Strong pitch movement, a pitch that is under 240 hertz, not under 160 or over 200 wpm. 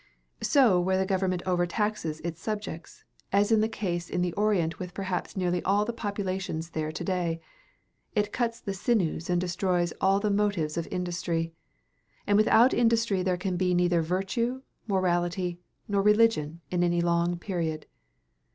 No: average, 3.0 semitones; medium, 185 Hz; average, 165 wpm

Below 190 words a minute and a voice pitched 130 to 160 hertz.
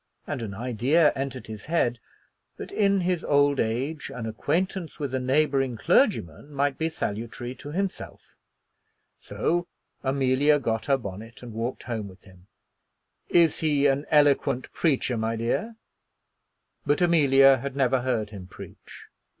Yes: average, 140 wpm; low, 135 Hz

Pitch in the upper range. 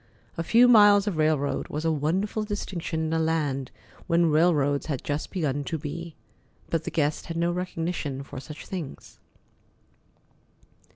No: medium, 160 Hz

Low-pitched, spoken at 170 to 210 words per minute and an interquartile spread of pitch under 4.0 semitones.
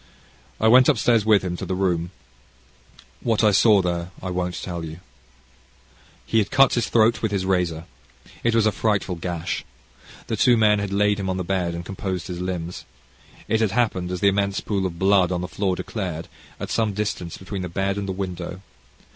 Yes: very low, 95 Hz; average, 200 wpm; average, 2.9 semitones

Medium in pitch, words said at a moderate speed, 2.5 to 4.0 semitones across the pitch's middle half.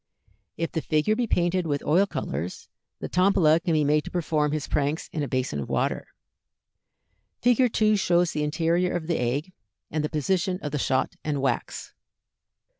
Yes: medium, 155 Hz; average, 180 wpm; average, 3.5 semitones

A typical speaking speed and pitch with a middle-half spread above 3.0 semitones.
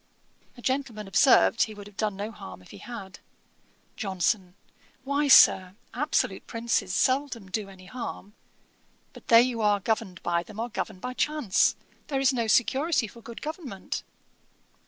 Yes: average, 155 wpm; average, 4.8 semitones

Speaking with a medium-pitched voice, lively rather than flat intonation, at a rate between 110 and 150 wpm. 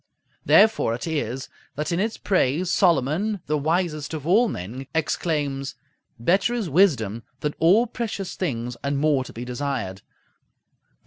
Yes: medium, 150 Hz; wide, 5.8 semitones; average, 145 wpm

